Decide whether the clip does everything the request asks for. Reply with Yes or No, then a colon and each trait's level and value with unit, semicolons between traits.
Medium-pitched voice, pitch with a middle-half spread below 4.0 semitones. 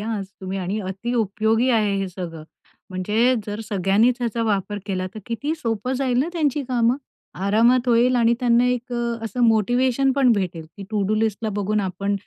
No: high, 225 Hz; average, 3.5 semitones